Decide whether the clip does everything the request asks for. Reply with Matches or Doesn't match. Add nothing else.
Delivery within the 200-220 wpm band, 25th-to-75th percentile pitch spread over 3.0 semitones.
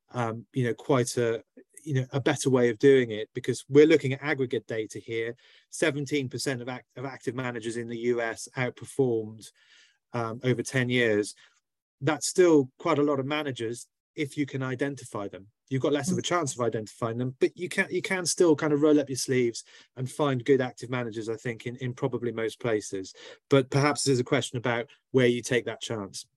Matches